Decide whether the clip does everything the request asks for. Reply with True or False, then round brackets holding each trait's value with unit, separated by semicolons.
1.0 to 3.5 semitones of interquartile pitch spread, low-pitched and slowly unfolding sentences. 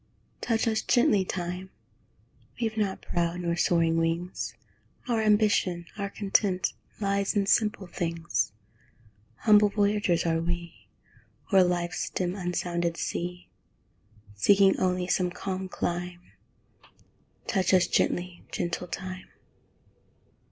False (2.5 semitones; 180 Hz; 110 wpm)